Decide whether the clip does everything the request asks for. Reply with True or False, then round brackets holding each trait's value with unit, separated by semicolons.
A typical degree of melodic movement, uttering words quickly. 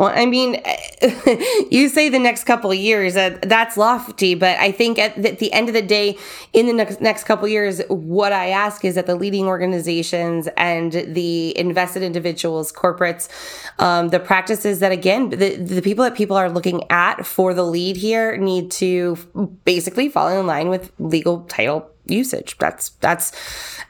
False (3.7 semitones; 180 wpm)